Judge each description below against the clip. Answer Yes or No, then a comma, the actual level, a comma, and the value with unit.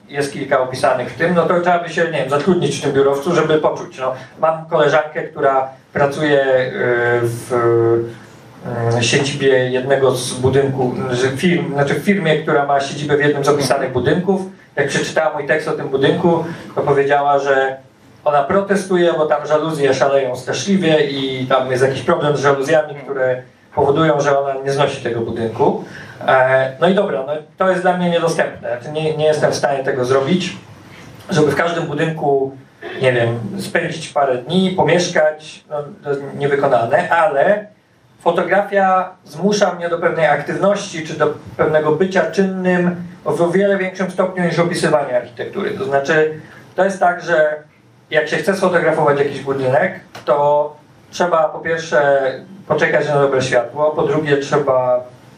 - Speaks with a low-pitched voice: No, medium, 150 Hz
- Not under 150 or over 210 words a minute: Yes, average, 155 wpm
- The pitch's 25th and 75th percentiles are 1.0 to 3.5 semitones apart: No, average, 3.9 semitones